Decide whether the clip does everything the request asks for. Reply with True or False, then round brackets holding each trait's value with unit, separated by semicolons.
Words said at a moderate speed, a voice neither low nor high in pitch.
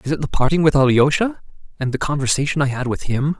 False (230 wpm; 145 Hz)